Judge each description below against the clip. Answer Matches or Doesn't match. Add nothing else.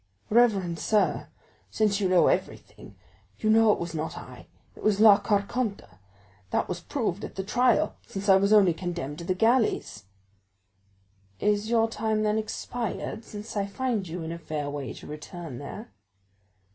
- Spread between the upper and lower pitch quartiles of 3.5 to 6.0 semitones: Matches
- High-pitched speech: Matches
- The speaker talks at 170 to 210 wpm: Doesn't match